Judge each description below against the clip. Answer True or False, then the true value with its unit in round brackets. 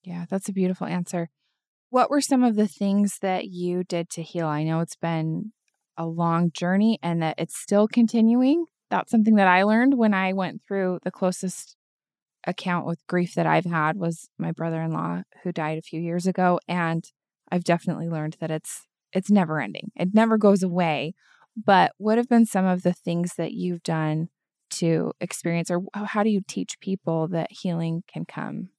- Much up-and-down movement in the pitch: False (3.3 semitones)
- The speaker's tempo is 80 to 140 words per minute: False (190 wpm)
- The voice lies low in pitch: False (180 Hz)